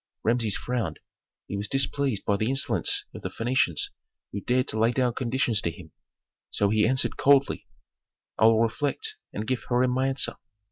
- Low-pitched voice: Yes, low, 120 Hz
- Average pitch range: Yes, average, 3.4 semitones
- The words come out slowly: No, average, 175 wpm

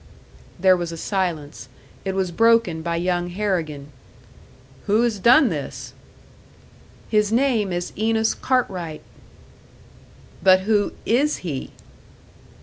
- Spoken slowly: Yes, slow, 110 wpm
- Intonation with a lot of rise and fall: No, average, 4.7 semitones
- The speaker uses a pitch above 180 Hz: Yes, high, 190 Hz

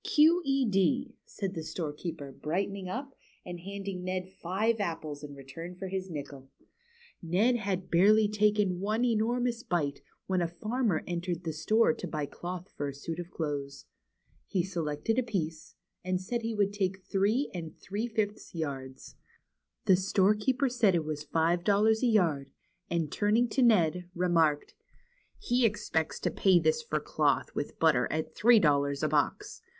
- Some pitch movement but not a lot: Yes, average, 4.8 semitones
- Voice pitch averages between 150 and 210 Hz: Yes, medium, 185 Hz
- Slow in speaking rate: No, average, 160 wpm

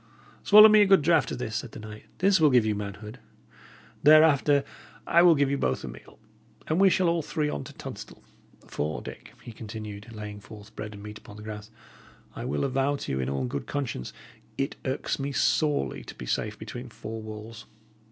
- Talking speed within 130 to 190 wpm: No, fast, 205 wpm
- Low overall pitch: Yes, low, 115 Hz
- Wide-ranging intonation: Yes, wide, 5.8 semitones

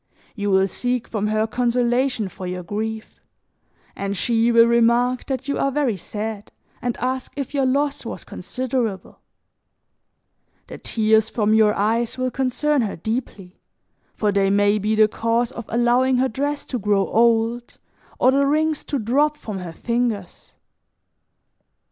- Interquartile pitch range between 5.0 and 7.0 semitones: No, average, 3.3 semitones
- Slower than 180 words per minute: Yes, average, 150 wpm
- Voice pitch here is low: No, high, 235 Hz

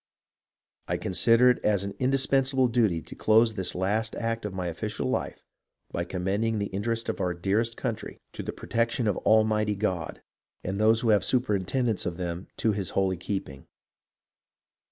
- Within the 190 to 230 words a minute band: No, average, 170 wpm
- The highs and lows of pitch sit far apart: No, average, 3.5 semitones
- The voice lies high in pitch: No, low, 105 Hz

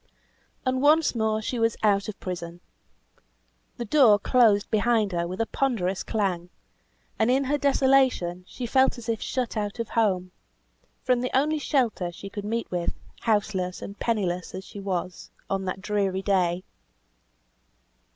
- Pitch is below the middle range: No, high, 210 Hz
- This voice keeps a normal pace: Yes, average, 155 wpm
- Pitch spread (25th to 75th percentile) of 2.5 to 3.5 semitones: No, average, 4.7 semitones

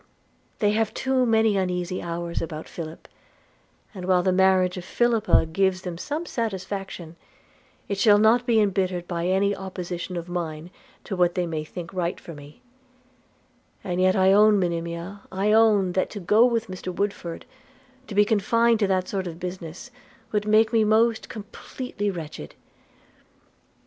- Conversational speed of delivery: Yes, average, 160 wpm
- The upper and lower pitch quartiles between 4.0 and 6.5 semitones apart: No, average, 3.3 semitones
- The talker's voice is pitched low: No, high, 190 Hz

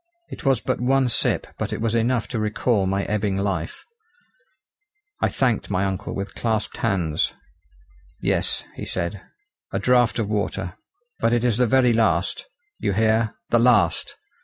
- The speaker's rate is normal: Yes, average, 160 wpm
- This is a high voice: No, low, 110 Hz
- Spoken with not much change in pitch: No, average, 3.6 semitones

